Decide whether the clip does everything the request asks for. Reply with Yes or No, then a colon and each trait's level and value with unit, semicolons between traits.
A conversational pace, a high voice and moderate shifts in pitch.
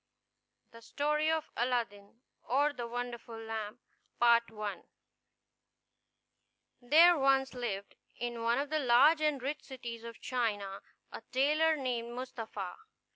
No: slow, 115 wpm; high, 245 Hz; average, 3.4 semitones